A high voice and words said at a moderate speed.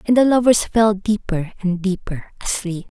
Yes: high, 200 Hz; average, 160 wpm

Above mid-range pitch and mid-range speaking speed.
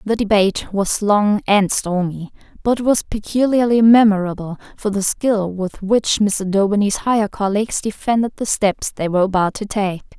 Yes: high, 205 Hz; average, 160 wpm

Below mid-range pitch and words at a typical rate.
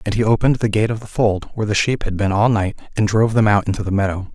No: low, 105 Hz; fast, 305 wpm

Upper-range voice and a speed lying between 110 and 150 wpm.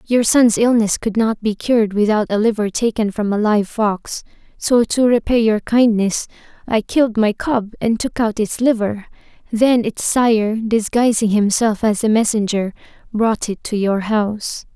No: high, 220 Hz; average, 170 wpm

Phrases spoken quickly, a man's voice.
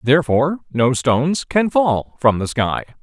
No: average, 160 wpm; male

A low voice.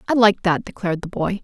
No: high, 195 Hz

